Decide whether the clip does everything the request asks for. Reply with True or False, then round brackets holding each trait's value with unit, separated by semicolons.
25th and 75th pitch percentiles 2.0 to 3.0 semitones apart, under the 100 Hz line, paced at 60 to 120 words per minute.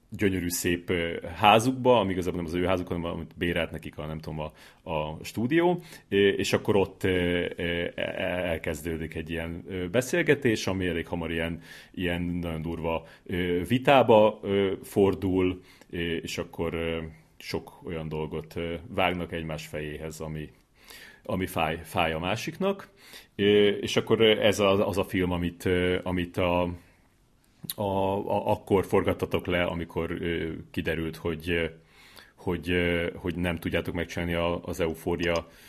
False (2.5 semitones; 90 Hz; 130 wpm)